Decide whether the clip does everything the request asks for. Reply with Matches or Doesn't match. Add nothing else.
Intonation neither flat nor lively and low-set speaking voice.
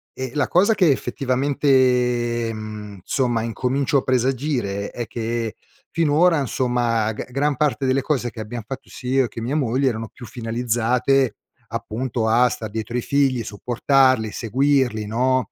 Matches